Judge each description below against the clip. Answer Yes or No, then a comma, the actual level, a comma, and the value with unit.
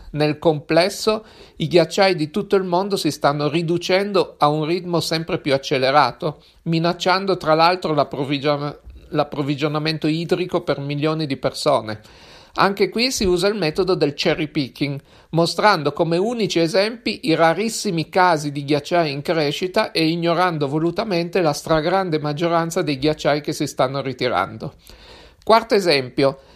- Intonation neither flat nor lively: Yes, average, 3.7 semitones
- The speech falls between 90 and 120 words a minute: No, average, 140 wpm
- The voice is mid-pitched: Yes, medium, 165 Hz